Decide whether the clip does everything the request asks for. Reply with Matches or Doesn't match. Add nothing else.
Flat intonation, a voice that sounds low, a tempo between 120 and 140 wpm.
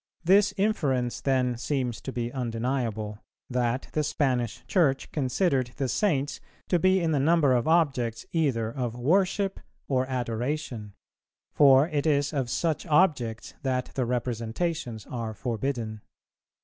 Doesn't match